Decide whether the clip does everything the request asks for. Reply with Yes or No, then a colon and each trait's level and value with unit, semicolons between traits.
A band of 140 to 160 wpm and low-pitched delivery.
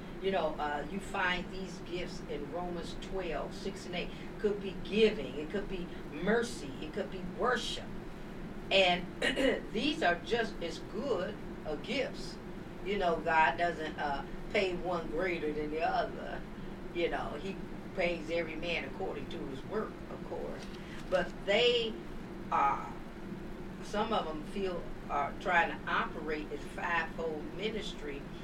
No: average, 150 wpm; medium, 185 Hz